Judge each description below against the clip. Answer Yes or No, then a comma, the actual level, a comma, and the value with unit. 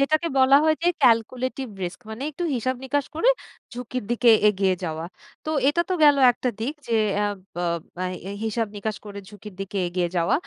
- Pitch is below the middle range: No, high, 230 Hz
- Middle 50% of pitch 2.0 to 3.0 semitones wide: No, average, 5.3 semitones